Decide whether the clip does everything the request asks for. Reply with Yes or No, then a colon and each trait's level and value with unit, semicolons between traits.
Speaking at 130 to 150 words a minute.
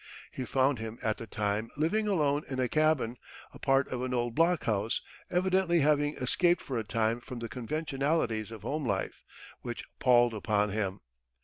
No: average, 175 wpm